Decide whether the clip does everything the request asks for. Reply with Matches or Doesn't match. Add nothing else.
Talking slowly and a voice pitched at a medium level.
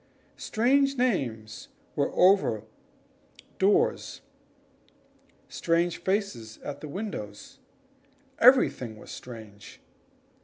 Matches